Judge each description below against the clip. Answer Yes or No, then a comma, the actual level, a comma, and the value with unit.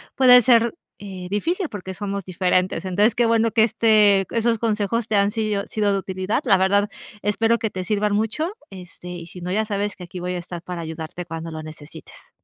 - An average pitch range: Yes, average, 3.5 semitones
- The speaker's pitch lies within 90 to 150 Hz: No, high, 200 Hz